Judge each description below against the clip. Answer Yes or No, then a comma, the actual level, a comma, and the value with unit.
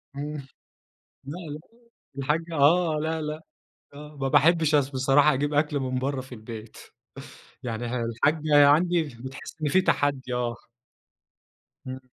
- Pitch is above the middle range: No, medium, 145 Hz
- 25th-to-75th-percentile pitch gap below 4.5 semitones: Yes, average, 2.9 semitones